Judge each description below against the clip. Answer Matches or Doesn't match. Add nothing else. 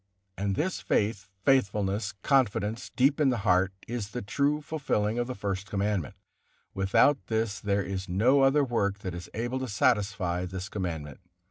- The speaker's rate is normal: Matches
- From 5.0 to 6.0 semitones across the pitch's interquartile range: Doesn't match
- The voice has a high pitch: Doesn't match